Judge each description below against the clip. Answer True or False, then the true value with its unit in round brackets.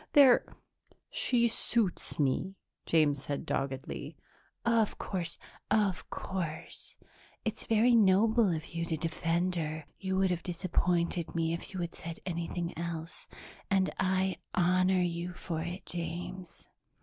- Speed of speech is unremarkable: False (130 wpm)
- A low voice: False (175 Hz)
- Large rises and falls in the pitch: False (2.4 semitones)